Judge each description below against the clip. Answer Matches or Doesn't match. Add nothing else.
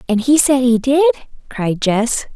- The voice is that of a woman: Matches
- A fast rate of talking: Doesn't match